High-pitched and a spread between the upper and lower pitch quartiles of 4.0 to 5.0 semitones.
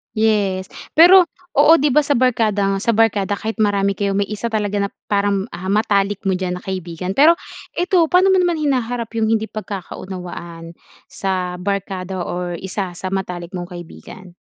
No: high, 200 Hz; average, 3.4 semitones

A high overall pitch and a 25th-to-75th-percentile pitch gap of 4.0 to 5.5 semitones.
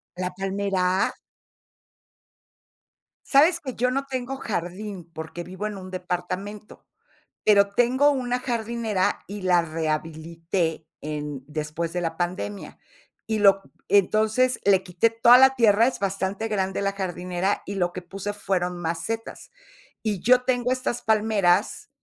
Yes: high, 195 Hz; average, 4.3 semitones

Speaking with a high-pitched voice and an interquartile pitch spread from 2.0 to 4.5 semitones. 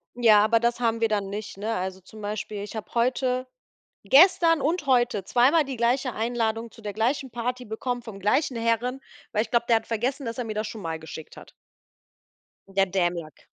Yes: high, 230 Hz; average, 3.1 semitones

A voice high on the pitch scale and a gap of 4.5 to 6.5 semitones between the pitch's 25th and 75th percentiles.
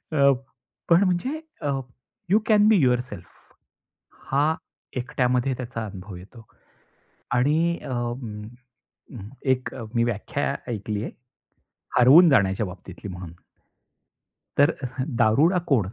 No: low, 125 Hz; average, 5.0 semitones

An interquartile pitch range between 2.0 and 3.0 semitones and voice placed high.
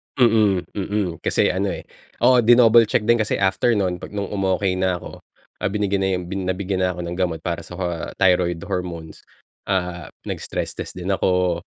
No: narrow, 2.4 semitones; very low, 95 Hz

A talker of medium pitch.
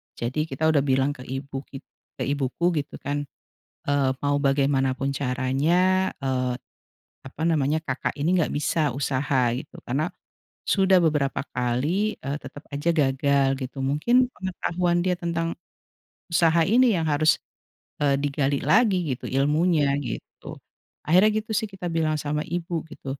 Yes: medium, 145 Hz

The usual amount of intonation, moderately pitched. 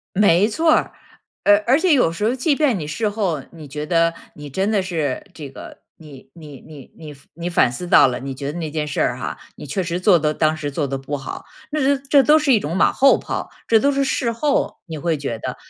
No: wide, 7.4 semitones; medium, 170 Hz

